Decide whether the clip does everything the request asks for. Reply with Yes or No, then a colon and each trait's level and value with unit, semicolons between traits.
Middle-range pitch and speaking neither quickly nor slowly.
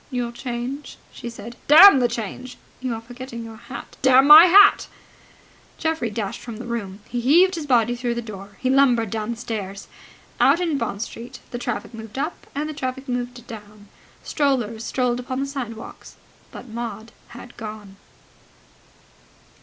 No: high, 240 Hz; average, 165 wpm